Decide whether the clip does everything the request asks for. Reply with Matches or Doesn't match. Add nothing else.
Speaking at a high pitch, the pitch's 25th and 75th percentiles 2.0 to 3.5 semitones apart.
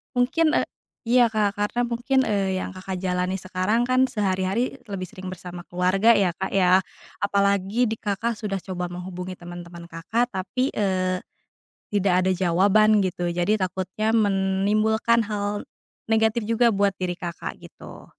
Matches